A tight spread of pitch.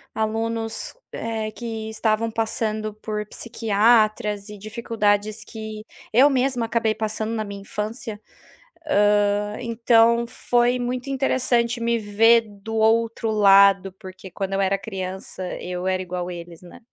Yes: narrow, 2.1 semitones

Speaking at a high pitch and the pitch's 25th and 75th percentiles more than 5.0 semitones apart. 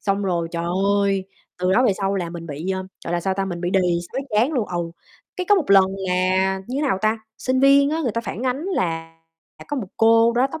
Yes: high, 195 Hz; wide, 5.5 semitones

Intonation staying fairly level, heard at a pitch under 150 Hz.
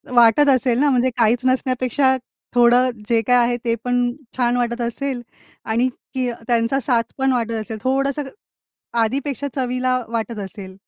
No: narrow, 1.9 semitones; high, 245 Hz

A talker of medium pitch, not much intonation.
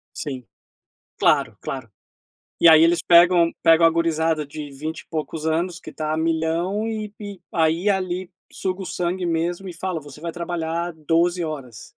Yes: medium, 165 Hz; narrow, 2.0 semitones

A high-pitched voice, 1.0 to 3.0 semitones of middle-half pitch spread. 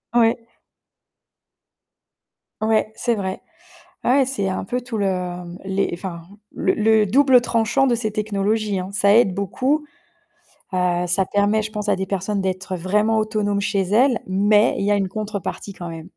Yes: high, 205 Hz; narrow, 2.6 semitones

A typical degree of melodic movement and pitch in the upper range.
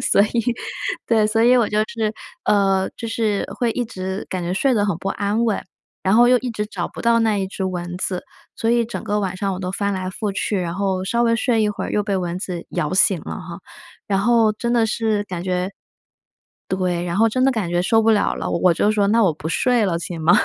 Yes: average, 3.5 semitones; high, 200 Hz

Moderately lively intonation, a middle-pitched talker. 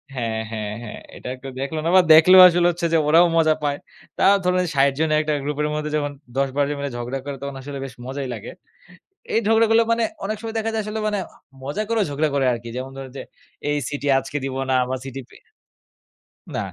Yes: average, 5.0 semitones; medium, 145 Hz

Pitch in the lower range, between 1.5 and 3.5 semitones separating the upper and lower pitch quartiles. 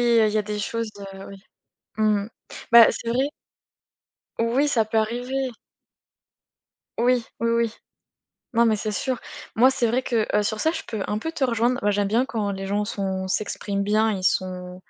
No: high, 220 Hz; average, 2.7 semitones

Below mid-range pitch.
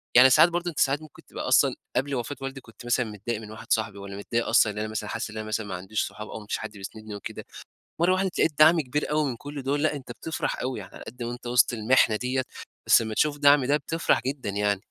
Yes: low, 125 Hz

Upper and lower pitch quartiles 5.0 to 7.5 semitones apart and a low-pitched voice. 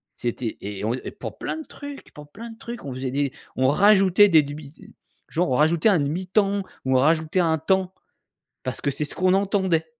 No: wide, 5.6 semitones; medium, 160 Hz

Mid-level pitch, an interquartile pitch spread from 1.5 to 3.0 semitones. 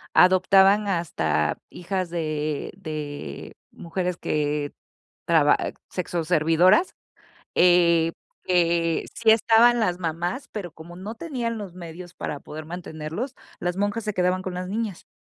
No: medium, 175 Hz; average, 3.4 semitones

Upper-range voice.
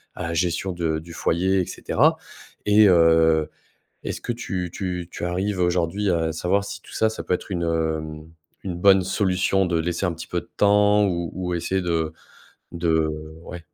No: very low, 90 Hz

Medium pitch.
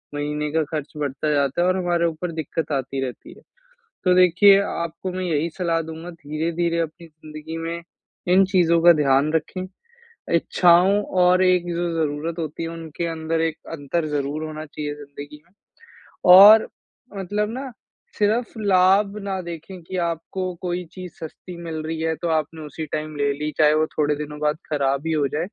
Yes: medium, 165 Hz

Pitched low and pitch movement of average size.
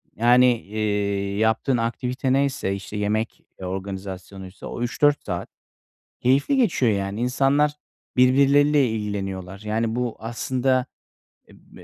Yes: low, 115 Hz; average, 4.6 semitones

